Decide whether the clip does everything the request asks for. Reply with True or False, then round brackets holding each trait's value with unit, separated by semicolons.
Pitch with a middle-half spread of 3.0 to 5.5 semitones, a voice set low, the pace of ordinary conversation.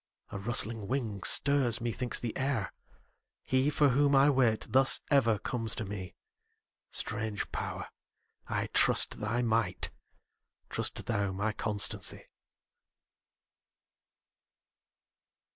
False (4.1 semitones; 115 Hz; 105 wpm)